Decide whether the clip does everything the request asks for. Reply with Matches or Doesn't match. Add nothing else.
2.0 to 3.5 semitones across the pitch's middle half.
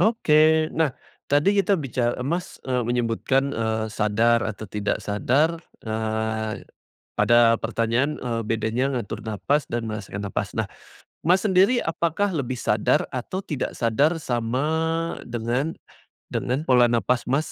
Doesn't match